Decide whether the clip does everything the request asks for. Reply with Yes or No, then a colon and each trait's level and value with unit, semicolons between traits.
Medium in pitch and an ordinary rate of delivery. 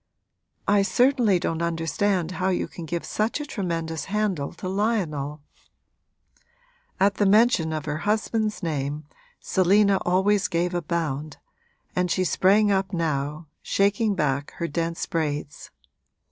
No: medium, 180 Hz; slow, 130 wpm